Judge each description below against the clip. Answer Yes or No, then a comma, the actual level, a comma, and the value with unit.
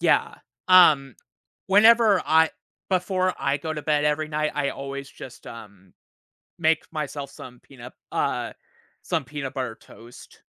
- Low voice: No, medium, 150 Hz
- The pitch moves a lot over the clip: No, average, 3.2 semitones